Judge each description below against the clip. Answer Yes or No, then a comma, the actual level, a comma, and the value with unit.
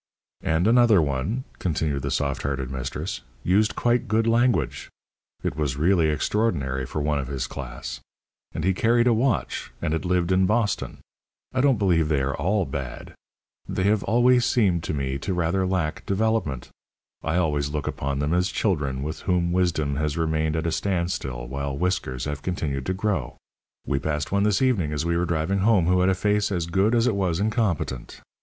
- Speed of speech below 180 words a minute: No, average, 190 wpm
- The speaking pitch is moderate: No, very low, 85 Hz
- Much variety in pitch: Yes, wide, 5.9 semitones